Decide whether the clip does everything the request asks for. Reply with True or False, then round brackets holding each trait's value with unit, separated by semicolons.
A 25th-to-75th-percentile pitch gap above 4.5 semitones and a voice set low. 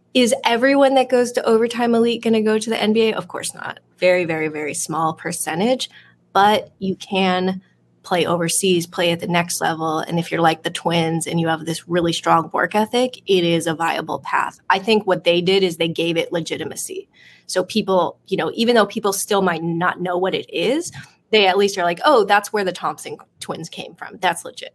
False (5.0 semitones; 185 Hz)